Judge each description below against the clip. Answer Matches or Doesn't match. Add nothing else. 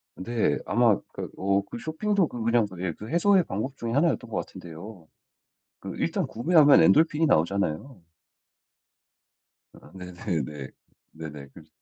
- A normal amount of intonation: Doesn't match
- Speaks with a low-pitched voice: Matches